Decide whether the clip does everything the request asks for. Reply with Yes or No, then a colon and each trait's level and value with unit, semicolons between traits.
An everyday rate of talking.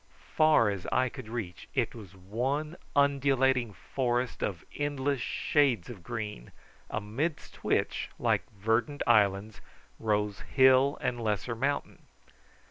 No: slow, 120 wpm